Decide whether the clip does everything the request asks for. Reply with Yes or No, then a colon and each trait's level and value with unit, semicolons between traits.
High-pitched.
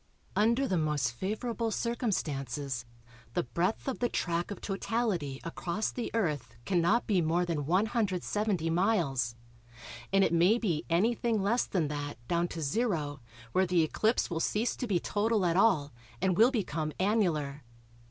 No: medium, 180 Hz